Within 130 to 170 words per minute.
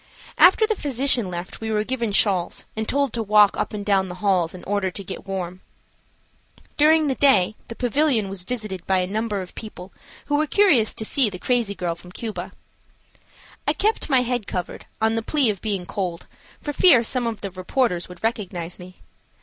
No: average, 200 wpm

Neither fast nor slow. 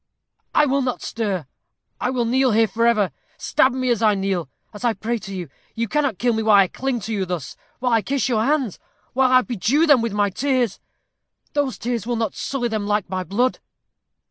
No: fast, 210 wpm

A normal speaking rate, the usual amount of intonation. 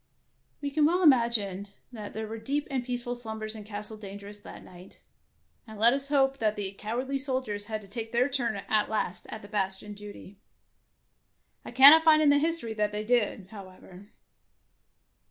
Yes: average, 175 wpm; average, 4.2 semitones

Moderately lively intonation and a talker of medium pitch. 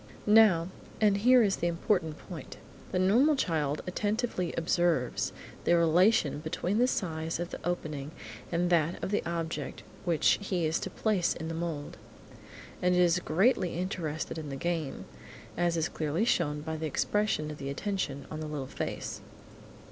Yes: average, 3.3 semitones; medium, 170 Hz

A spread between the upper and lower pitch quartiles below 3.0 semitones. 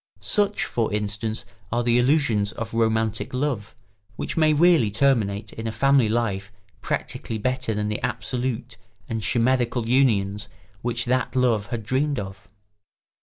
No: average, 3.3 semitones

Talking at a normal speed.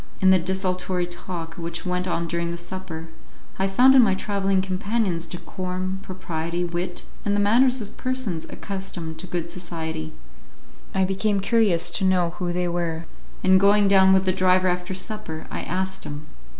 Yes: average, 170 wpm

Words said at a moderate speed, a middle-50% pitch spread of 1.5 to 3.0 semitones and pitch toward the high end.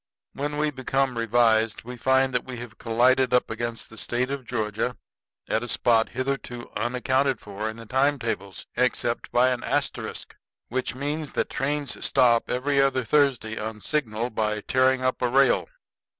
No: average, 165 wpm; narrow, 2.6 semitones; low, 125 Hz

